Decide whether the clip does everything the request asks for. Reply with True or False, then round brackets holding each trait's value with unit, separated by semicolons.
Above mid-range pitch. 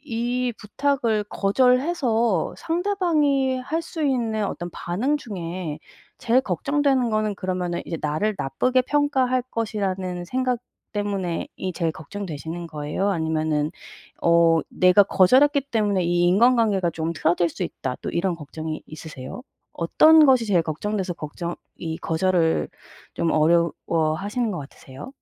True (195 Hz)